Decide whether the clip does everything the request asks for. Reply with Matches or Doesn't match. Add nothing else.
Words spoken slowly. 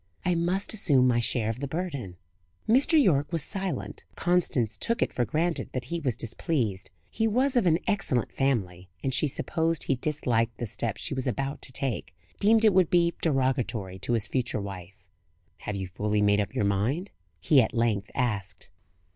Doesn't match